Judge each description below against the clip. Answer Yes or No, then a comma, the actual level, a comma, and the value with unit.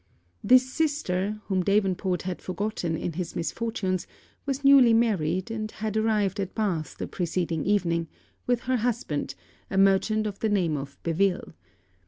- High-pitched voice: Yes, high, 195 Hz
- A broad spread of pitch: No, average, 3.9 semitones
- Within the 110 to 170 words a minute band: Yes, average, 150 wpm